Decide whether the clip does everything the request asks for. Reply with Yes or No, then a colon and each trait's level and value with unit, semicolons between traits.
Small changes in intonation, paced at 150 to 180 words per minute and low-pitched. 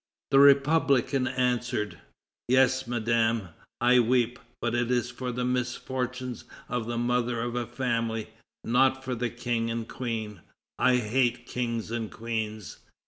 No: narrow, 1.5 semitones; average, 140 wpm; low, 120 Hz